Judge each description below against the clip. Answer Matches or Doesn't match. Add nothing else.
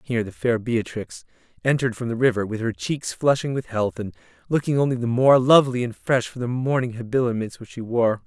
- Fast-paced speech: Matches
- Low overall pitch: Matches